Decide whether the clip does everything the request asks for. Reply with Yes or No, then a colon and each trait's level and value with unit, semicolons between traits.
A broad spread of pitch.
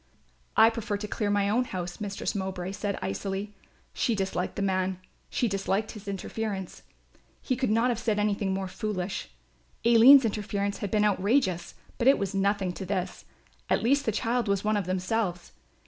No: average, 2.7 semitones